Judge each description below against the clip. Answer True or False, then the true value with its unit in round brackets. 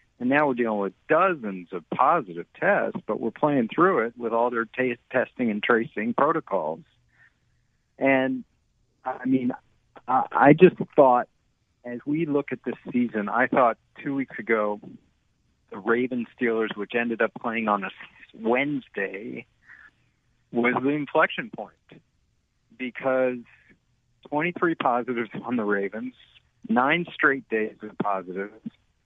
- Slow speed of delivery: True (130 wpm)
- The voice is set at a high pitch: False (120 Hz)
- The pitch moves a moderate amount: True (3.5 semitones)